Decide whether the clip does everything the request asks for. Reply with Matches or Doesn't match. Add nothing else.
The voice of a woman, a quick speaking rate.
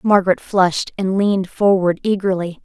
Doesn't match